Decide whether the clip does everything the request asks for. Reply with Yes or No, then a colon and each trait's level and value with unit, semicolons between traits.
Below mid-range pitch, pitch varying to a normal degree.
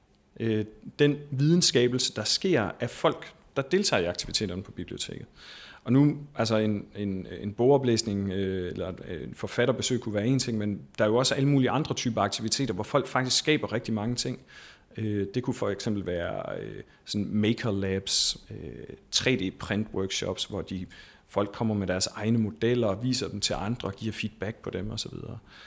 Yes: low, 110 Hz; average, 3.8 semitones